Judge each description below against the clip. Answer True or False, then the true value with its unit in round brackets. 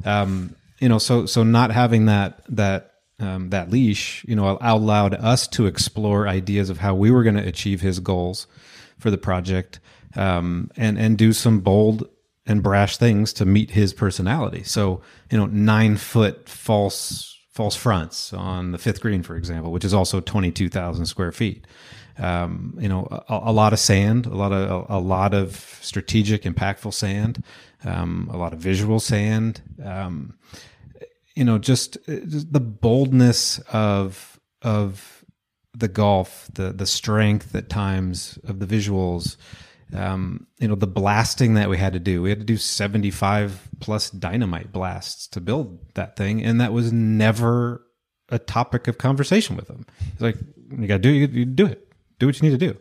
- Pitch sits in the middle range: False (105 Hz)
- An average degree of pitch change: True (3.2 semitones)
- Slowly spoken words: False (180 wpm)